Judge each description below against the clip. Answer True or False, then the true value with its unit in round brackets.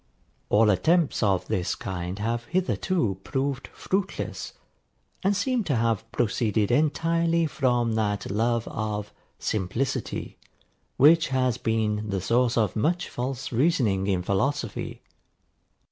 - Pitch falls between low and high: False (115 Hz)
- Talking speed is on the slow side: True (115 wpm)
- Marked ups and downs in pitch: True (5.8 semitones)